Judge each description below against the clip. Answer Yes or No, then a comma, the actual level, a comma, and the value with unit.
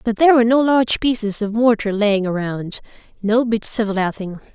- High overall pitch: Yes, high, 220 Hz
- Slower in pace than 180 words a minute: Yes, average, 170 wpm